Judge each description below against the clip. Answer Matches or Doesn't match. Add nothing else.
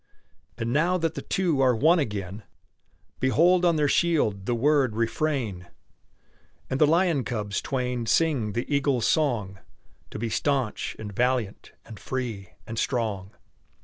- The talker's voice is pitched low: Matches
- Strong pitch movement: Matches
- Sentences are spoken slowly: Doesn't match